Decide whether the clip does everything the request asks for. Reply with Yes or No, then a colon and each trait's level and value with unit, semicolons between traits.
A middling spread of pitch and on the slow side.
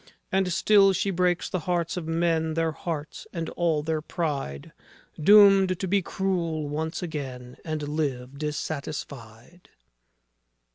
Yes: average, 3.3 semitones; slow, 130 wpm